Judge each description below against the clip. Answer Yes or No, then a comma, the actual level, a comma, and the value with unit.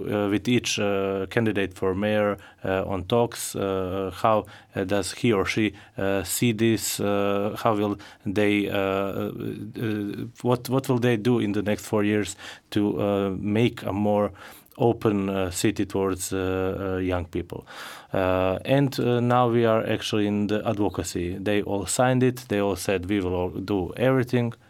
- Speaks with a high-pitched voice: No, low, 105 Hz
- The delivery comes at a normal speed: Yes, average, 175 wpm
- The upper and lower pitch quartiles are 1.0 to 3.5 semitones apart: Yes, average, 2.8 semitones